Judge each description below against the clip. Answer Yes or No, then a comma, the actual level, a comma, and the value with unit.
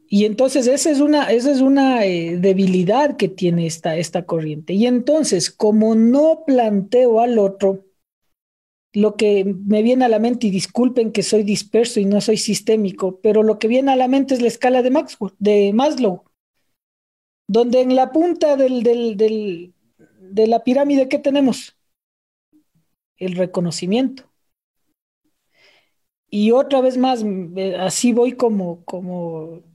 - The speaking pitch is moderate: No, high, 220 Hz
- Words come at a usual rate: Yes, average, 150 wpm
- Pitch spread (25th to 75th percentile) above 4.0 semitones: Yes, average, 5.0 semitones